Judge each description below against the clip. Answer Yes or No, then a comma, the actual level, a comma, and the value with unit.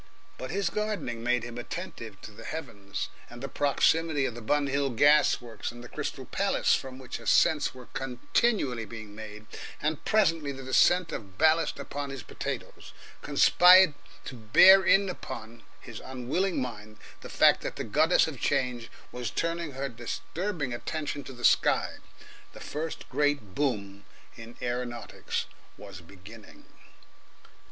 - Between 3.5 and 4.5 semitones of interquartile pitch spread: No, average, 5.2 semitones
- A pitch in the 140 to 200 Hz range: No, low, 130 Hz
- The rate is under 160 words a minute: Yes, average, 150 wpm